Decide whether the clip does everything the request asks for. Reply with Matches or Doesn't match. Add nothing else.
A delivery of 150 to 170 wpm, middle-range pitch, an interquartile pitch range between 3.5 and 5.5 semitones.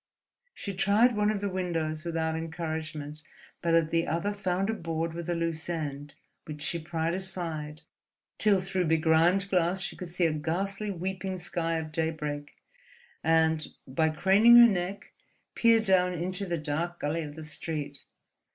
Doesn't match